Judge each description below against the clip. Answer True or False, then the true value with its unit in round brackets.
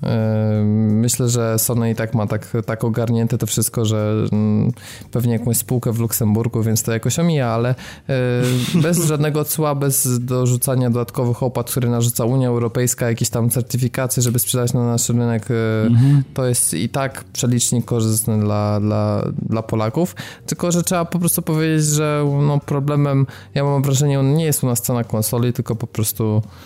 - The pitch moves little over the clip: False (3.1 semitones)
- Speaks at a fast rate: True (165 wpm)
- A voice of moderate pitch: False (120 Hz)